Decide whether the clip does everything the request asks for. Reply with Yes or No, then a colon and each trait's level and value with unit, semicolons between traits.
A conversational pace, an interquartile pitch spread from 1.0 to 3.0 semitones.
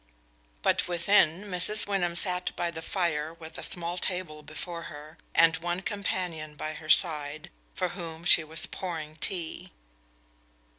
Yes: average, 145 wpm; narrow, 2.4 semitones